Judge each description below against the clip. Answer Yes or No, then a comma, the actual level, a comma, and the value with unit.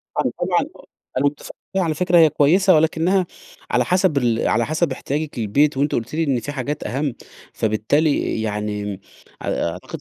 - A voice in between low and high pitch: Yes, medium, 145 Hz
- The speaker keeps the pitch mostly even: No, wide, 5.4 semitones